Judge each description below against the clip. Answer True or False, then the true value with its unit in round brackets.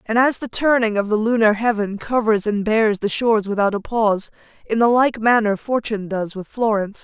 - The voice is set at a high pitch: True (220 Hz)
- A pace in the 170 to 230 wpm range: True (205 wpm)